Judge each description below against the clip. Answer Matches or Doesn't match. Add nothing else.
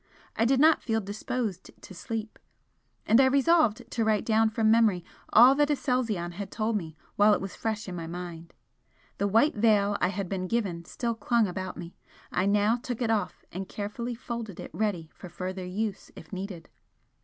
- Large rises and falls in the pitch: Doesn't match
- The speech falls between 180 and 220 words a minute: Matches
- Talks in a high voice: Matches